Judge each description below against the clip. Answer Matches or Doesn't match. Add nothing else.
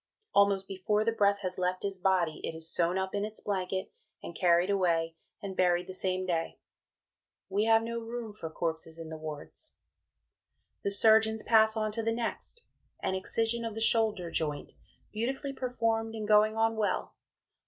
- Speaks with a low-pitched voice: Doesn't match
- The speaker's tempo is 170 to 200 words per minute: Matches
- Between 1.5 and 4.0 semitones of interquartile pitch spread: Matches